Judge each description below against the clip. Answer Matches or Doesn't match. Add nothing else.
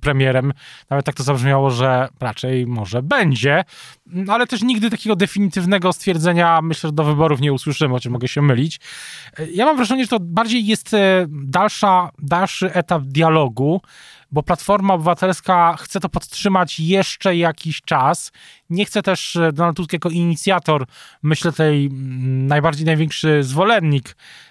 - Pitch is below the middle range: Doesn't match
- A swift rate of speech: Doesn't match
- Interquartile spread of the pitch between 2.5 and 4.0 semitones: Doesn't match